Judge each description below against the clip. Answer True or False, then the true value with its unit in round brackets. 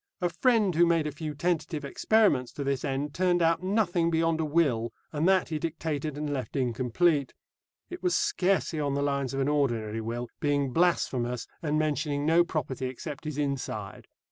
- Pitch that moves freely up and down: False (3.7 semitones)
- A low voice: False (150 Hz)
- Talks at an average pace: True (180 wpm)